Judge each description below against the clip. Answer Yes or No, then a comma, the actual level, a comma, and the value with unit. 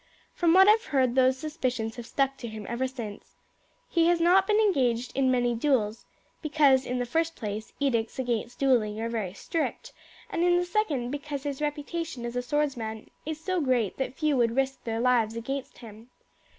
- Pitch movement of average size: Yes, average, 4.5 semitones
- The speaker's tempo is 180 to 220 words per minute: Yes, average, 190 wpm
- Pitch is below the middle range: No, very high, 260 Hz